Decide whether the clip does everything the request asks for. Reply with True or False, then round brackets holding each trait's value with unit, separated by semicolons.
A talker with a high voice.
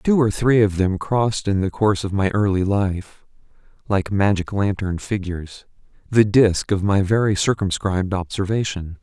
False (100 Hz)